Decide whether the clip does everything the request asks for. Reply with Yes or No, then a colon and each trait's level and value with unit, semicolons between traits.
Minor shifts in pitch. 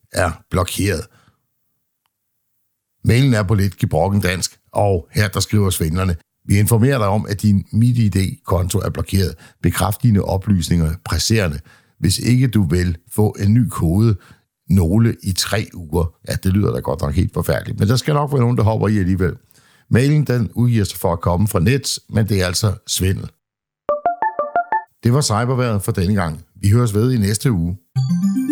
No: average, 4.5 semitones